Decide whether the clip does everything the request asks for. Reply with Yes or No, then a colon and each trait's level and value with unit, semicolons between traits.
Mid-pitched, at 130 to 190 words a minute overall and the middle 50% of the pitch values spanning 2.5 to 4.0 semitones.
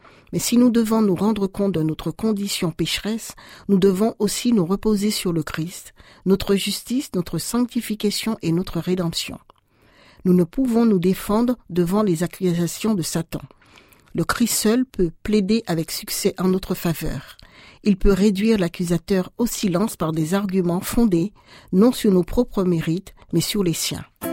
No: high, 195 Hz; average, 160 wpm; average, 3.7 semitones